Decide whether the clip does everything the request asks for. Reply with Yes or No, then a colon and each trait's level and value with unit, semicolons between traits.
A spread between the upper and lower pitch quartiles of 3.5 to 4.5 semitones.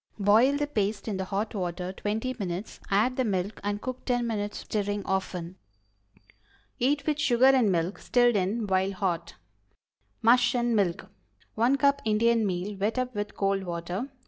Yes: average, 4.1 semitones